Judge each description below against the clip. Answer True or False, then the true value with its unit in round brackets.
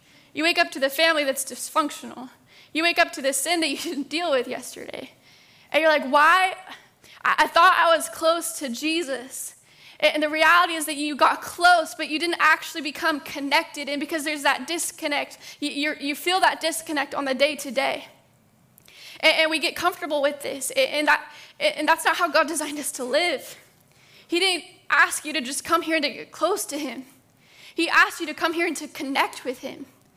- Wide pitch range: False (2.5 semitones)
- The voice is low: False (310 Hz)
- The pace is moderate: True (195 wpm)